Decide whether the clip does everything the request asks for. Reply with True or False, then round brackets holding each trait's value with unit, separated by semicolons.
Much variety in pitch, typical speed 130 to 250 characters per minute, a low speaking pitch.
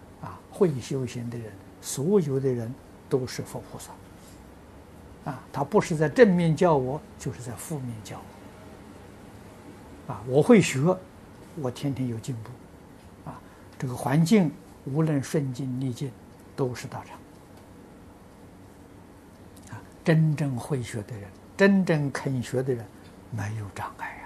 True (6.4 semitones; 180 characters per minute; 125 Hz)